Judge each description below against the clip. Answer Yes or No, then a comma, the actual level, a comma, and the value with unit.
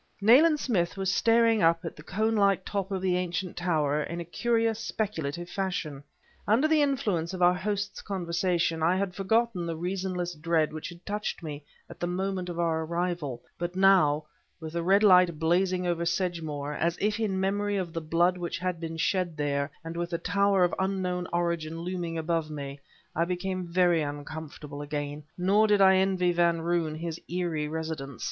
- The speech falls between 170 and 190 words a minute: Yes, average, 185 wpm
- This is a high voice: No, medium, 175 Hz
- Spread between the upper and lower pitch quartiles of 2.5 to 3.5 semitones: Yes, average, 2.8 semitones